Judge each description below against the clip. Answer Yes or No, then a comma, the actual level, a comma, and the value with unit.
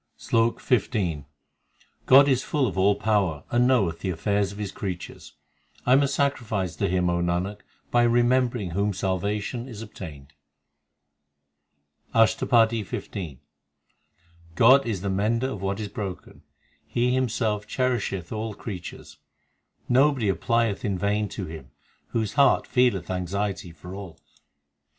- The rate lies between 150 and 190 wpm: No, average, 140 wpm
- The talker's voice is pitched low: Yes, low, 105 Hz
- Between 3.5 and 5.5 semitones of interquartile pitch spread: Yes, average, 4.3 semitones